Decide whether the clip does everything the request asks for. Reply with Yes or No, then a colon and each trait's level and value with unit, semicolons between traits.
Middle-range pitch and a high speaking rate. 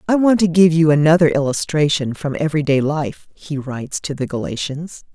No: medium, 155 Hz; average, 175 wpm